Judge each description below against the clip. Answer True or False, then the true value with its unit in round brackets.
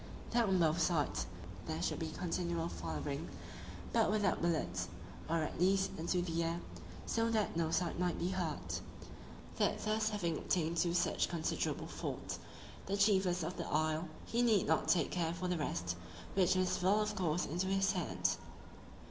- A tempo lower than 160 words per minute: False (170 wpm)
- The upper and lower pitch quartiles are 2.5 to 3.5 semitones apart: True (2.9 semitones)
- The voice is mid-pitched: True (175 Hz)